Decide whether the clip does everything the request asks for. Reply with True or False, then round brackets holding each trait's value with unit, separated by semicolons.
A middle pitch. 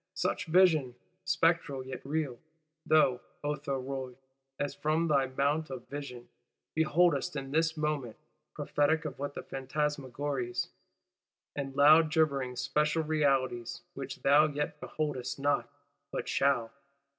True (145 Hz)